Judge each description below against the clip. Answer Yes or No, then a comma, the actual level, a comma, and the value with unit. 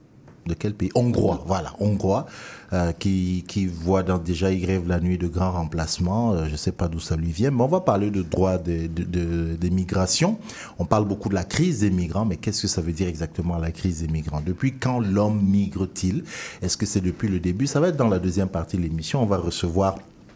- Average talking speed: No, fast, 235 wpm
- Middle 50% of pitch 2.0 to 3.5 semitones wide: Yes, average, 3.0 semitones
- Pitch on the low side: Yes, very low, 95 Hz